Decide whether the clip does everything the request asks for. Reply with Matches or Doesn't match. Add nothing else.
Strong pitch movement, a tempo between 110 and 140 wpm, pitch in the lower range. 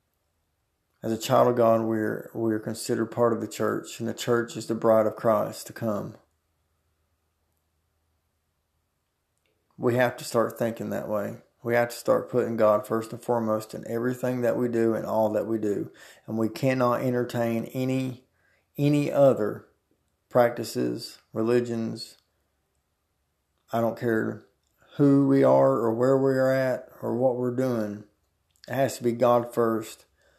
Doesn't match